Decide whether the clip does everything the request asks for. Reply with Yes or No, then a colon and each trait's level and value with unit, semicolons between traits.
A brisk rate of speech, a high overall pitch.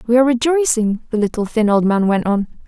Yes: fast, 225 wpm; high, 230 Hz